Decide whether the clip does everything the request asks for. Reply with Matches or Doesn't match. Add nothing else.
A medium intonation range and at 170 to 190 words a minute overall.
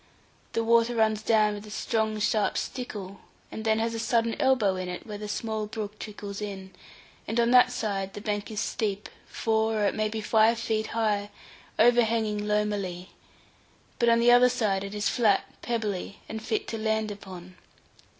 Doesn't match